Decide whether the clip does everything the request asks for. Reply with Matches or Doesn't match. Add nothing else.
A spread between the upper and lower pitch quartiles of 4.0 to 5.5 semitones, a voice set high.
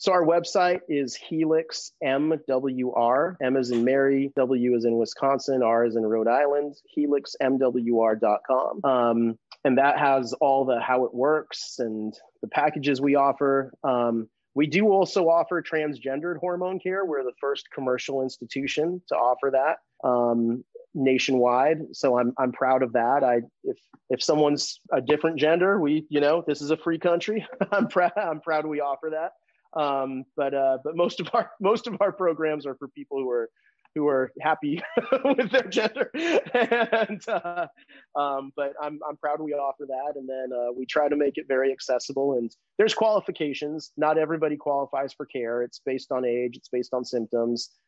Doesn't match